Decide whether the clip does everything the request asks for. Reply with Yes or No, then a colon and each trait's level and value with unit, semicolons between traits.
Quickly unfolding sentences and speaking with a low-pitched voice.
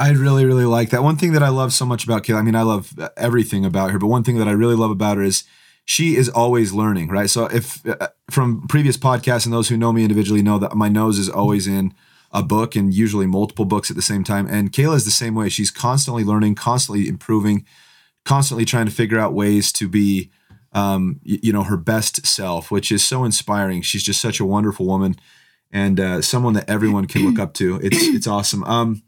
Yes: fast, 235 wpm; low, 110 Hz